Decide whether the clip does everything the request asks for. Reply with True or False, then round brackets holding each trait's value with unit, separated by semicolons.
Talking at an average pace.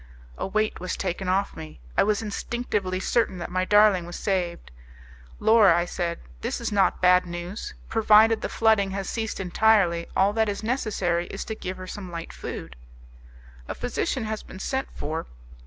True (175 wpm)